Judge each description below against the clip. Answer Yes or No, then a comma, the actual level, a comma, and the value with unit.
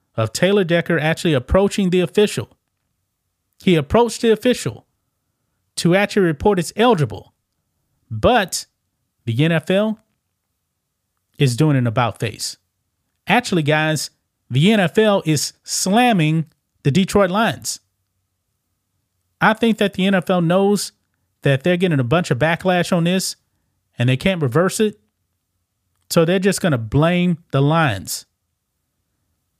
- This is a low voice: No, medium, 155 Hz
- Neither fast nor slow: No, slow, 120 wpm